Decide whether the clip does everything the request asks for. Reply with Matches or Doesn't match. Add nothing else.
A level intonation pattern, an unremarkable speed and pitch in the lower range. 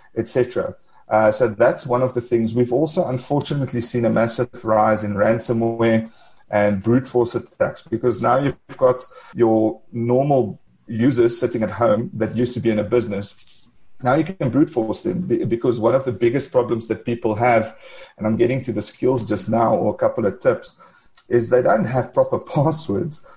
Matches